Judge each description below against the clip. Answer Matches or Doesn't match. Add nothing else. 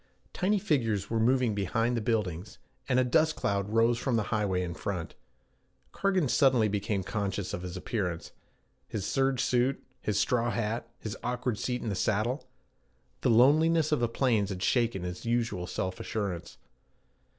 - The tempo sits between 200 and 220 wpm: Doesn't match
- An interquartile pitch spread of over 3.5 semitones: Matches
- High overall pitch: Doesn't match